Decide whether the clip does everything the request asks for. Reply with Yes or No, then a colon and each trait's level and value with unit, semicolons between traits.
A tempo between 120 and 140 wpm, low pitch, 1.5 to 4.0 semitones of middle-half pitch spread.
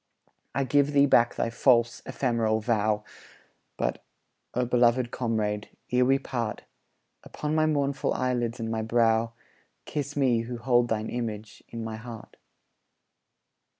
Yes: slow, 135 wpm; low, 120 Hz; narrow, 2.4 semitones